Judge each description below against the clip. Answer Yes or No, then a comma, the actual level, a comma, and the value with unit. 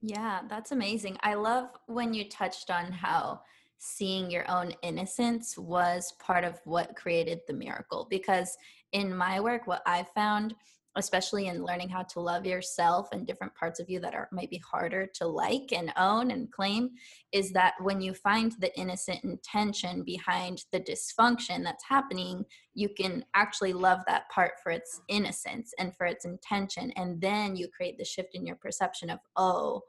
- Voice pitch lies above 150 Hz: Yes, high, 190 Hz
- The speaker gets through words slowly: No, average, 175 wpm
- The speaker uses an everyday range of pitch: Yes, average, 3.6 semitones